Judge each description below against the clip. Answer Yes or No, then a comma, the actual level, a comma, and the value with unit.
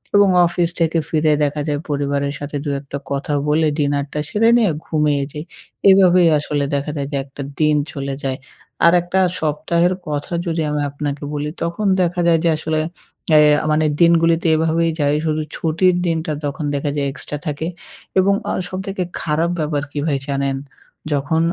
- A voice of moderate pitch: Yes, medium, 155 Hz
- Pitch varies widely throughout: No, narrow, 2.6 semitones